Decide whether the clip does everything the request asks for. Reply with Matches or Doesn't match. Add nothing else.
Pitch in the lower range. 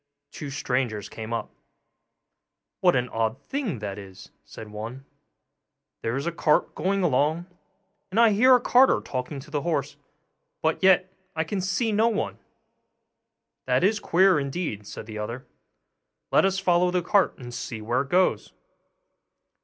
Doesn't match